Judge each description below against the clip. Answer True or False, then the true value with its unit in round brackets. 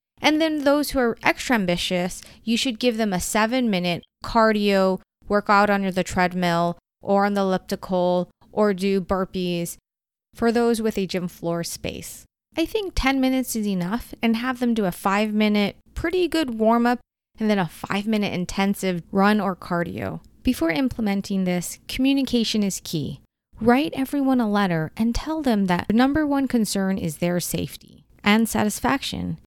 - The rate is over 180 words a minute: False (160 wpm)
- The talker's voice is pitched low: False (210 Hz)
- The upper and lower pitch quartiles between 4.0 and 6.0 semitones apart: True (4.7 semitones)